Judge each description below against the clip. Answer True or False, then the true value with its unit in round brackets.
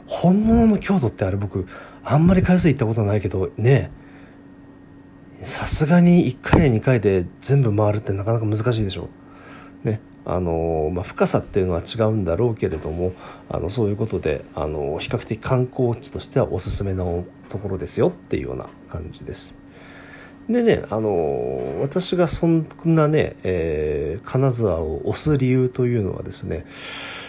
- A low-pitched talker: True (120 Hz)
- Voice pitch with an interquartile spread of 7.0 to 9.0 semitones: True (7.9 semitones)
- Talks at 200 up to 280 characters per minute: False (315 characters per minute)